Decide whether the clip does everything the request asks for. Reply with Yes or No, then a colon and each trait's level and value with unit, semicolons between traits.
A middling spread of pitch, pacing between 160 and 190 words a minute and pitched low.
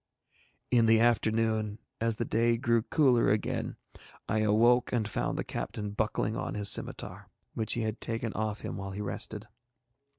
No: narrow, 1.6 semitones; average, 165 wpm; low, 110 Hz